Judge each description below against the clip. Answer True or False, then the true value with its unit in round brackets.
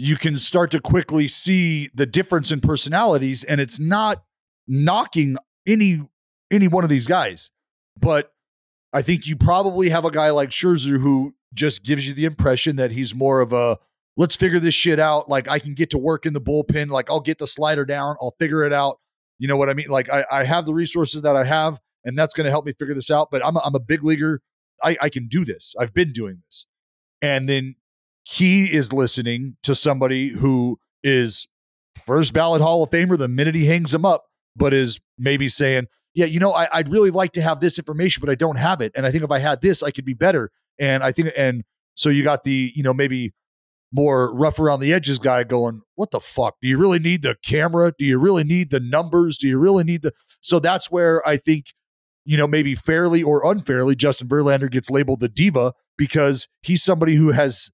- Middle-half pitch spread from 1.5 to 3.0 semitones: False (3.5 semitones)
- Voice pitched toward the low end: False (145 Hz)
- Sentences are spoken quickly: True (225 wpm)